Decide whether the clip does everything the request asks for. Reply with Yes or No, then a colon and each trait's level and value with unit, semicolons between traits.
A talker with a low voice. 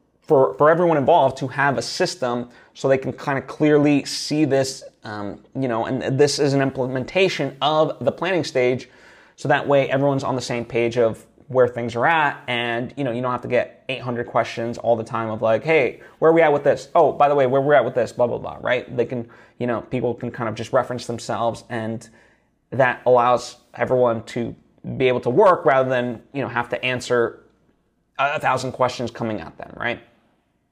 Yes: low, 125 Hz